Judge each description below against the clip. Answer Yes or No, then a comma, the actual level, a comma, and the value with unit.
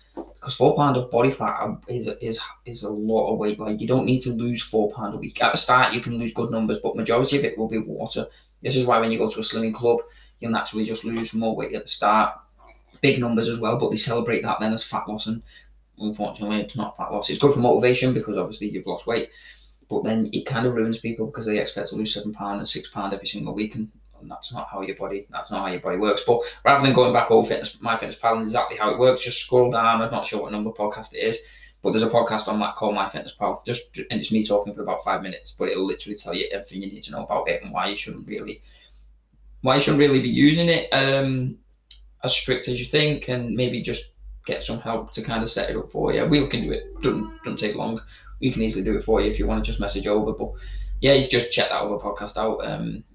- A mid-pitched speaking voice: No, low, 115 Hz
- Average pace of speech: No, fast, 270 wpm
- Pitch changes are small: No, average, 3.0 semitones